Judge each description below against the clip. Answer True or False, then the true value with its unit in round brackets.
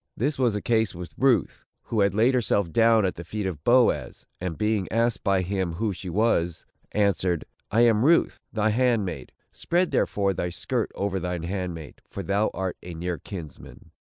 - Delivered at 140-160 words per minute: False (185 wpm)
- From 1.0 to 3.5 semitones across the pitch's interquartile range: False (4.1 semitones)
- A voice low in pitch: True (100 Hz)